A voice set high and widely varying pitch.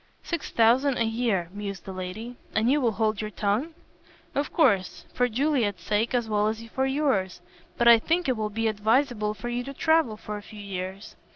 No: high, 225 Hz; average, 3.6 semitones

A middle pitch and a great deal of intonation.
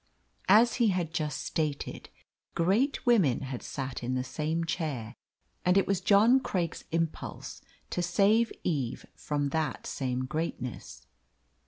Yes: medium, 160 Hz; wide, 6.5 semitones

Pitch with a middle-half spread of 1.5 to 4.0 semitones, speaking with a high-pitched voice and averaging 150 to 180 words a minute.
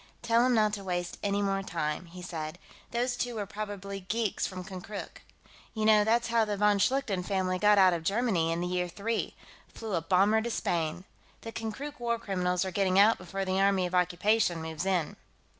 No: average, 3.3 semitones; high, 195 Hz; average, 200 wpm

